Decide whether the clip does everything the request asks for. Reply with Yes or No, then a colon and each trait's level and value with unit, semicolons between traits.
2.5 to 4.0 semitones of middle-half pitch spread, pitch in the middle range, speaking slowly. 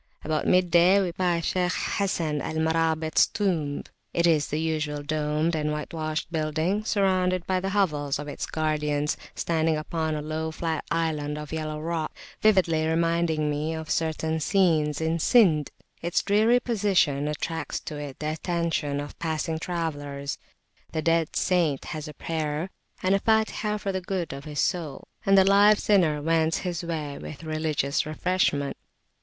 No: average, 2.9 semitones; medium, 160 Hz; average, 160 wpm